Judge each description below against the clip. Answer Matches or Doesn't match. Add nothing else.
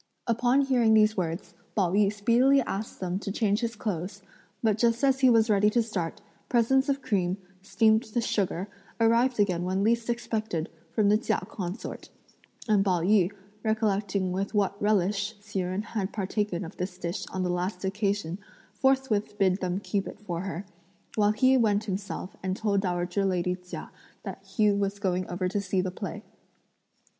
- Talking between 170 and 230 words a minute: Matches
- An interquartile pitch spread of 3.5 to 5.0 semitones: Doesn't match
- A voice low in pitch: Doesn't match